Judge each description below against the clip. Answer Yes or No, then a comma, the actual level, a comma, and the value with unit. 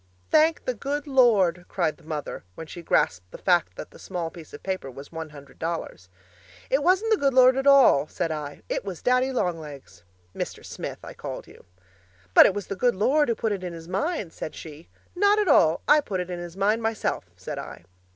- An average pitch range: No, wide, 8.1 semitones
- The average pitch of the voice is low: No, medium, 185 Hz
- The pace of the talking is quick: Yes, fast, 220 wpm